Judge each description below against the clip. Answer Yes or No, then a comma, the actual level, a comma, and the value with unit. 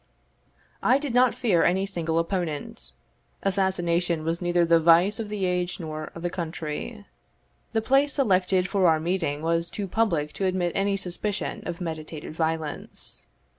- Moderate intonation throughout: Yes, average, 3.2 semitones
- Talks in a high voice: No, medium, 175 Hz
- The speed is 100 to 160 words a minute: Yes, average, 155 wpm